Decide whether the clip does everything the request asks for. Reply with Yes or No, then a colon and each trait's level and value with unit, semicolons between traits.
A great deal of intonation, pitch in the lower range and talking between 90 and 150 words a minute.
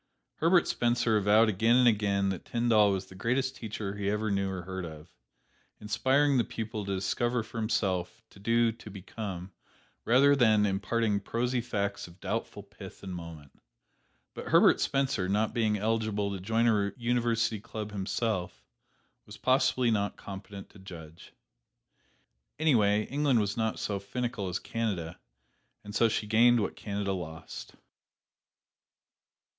No: average, 3.1 semitones; low, 105 Hz; average, 145 wpm